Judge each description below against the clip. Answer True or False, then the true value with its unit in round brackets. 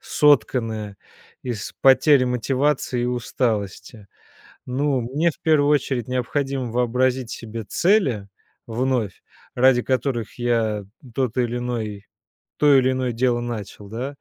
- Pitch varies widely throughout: False (2.6 semitones)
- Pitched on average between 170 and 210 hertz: False (125 Hz)